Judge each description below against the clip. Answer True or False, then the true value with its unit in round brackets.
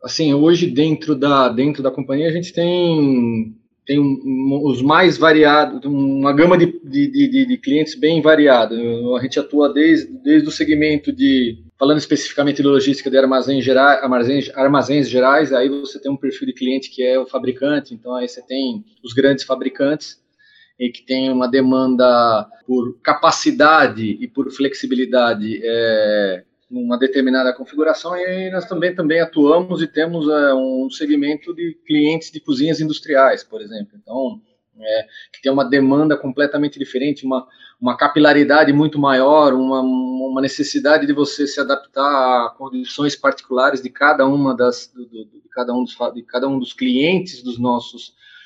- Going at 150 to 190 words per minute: True (160 wpm)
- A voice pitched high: False (140 Hz)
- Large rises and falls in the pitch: False (3.2 semitones)